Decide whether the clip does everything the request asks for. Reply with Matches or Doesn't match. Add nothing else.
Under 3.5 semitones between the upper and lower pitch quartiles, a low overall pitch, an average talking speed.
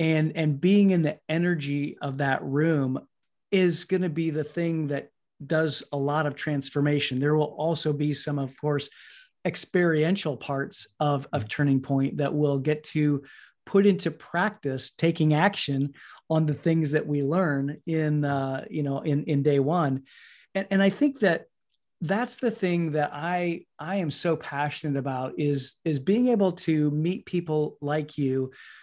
Doesn't match